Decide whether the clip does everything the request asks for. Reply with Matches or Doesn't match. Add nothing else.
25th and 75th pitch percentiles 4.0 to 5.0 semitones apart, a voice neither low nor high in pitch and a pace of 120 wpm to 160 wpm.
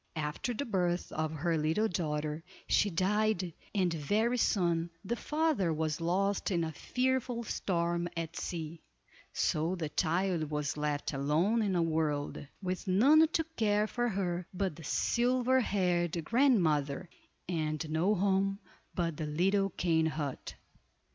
Matches